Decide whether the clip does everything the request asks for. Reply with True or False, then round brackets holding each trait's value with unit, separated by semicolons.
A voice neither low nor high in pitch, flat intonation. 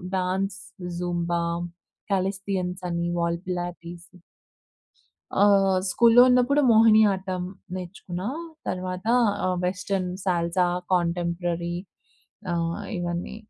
True (180 Hz; 1.9 semitones)